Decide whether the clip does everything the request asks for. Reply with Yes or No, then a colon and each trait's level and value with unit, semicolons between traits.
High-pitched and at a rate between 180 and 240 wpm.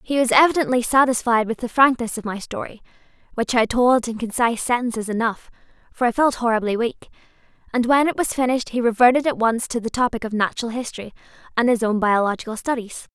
Yes: high, 235 Hz; average, 190 wpm